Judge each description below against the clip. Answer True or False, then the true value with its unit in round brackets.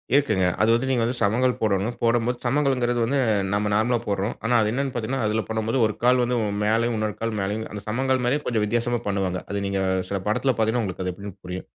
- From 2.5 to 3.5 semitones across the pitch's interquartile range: True (2.9 semitones)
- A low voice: True (115 Hz)